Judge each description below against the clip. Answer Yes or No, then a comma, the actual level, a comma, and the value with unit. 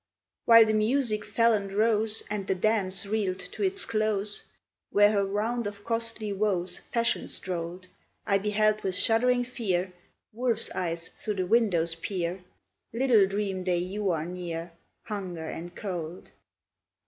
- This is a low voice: No, high, 205 Hz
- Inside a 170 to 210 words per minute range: No, average, 145 wpm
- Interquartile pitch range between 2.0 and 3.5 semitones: Yes, average, 3.2 semitones